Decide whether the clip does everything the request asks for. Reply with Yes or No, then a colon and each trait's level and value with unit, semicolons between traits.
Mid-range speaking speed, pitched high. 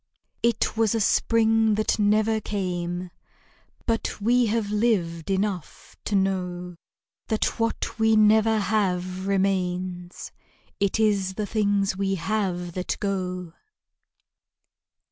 No: slow, 110 wpm; high, 200 Hz